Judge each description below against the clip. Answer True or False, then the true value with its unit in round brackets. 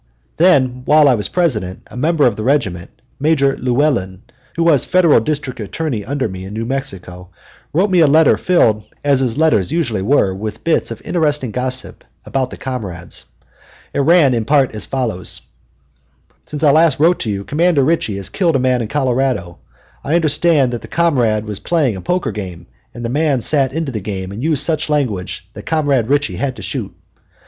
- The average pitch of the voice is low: True (130 Hz)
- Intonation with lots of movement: True (6.2 semitones)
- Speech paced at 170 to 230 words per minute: True (190 wpm)